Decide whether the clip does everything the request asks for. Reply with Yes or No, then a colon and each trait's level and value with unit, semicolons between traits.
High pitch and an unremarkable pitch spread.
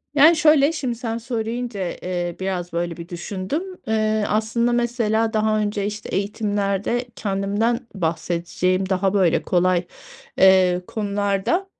Yes: high, 205 Hz; average, 3.8 semitones